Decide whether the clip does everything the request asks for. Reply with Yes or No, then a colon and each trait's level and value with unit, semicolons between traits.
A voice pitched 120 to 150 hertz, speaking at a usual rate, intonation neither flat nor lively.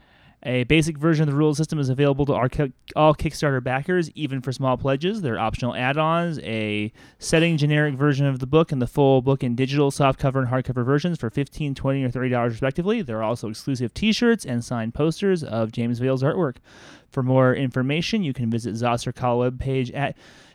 Yes: low, 135 Hz; average, 190 wpm; average, 3.4 semitones